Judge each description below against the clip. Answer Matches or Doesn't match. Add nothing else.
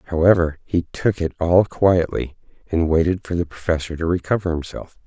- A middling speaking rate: Matches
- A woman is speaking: Doesn't match